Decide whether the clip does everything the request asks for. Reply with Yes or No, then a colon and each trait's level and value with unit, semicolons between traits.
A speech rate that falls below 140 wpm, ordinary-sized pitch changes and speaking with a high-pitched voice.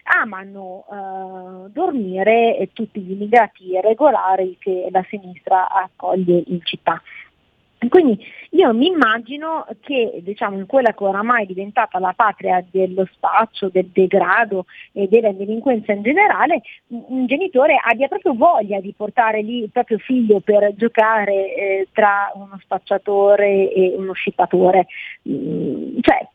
Yes: average, 130 wpm; average, 3.8 semitones; high, 205 Hz